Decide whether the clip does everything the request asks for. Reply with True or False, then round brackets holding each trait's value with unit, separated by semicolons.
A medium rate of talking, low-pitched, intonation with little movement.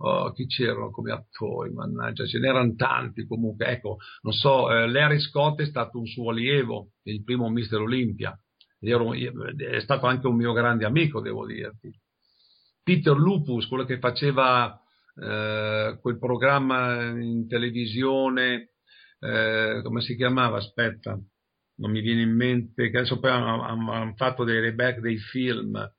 True (150 wpm; 120 Hz; 2.1 semitones)